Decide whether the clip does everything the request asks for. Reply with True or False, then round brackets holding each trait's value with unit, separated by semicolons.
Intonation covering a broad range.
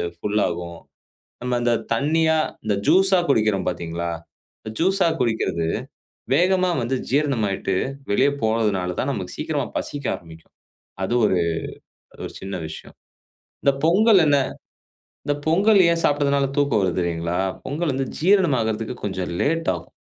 True (8.8 semitones)